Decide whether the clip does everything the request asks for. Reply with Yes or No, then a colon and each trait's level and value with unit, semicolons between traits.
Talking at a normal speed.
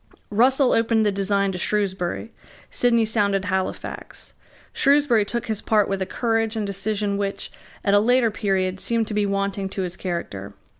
Yes: average, 165 wpm